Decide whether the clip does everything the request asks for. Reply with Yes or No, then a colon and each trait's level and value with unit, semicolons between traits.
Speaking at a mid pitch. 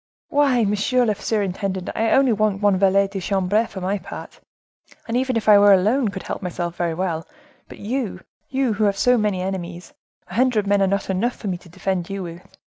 No: high, 200 Hz